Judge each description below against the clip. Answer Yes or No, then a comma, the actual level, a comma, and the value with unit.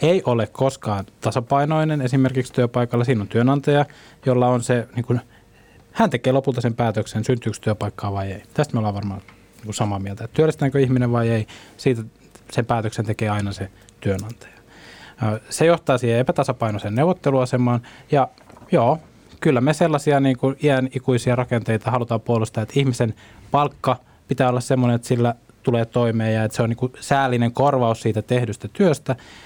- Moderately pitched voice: No, low, 120 Hz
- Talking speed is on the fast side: Yes, fast, 160 wpm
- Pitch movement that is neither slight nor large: Yes, average, 3.1 semitones